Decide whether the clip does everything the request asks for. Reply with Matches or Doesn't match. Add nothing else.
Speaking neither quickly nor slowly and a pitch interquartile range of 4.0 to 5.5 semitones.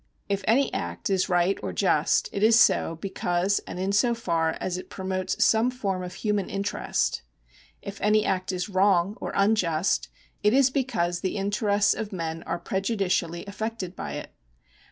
Doesn't match